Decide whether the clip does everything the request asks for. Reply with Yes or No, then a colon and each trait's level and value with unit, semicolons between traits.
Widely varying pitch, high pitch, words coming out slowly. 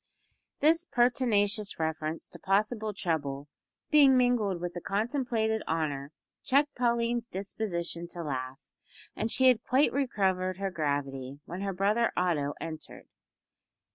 Yes: wide, 6.5 semitones; high, 195 Hz; slow, 125 wpm